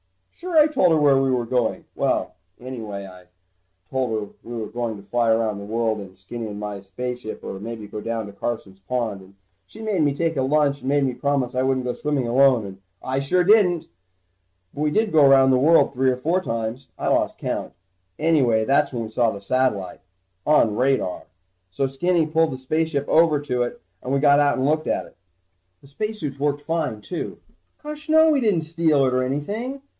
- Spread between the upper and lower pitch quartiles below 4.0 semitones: No, average, 5.3 semitones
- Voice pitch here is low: Yes, low, 130 Hz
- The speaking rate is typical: No, fast, 210 wpm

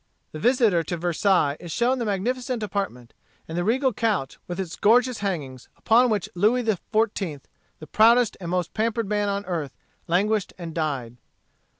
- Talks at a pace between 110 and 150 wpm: No, average, 165 wpm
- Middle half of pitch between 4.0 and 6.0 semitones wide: Yes, average, 5.2 semitones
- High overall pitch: Yes, high, 200 Hz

